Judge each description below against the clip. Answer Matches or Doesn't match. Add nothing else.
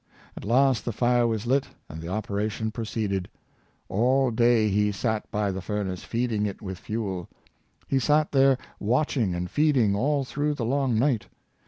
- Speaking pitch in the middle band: Doesn't match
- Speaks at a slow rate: Doesn't match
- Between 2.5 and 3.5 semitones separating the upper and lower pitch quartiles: Doesn't match